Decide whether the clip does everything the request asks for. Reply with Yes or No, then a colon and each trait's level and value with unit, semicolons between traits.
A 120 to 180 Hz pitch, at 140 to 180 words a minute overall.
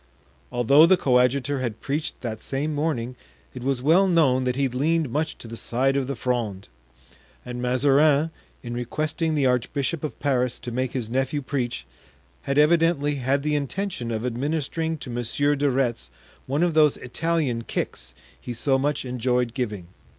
Yes: low, 135 Hz; average, 165 wpm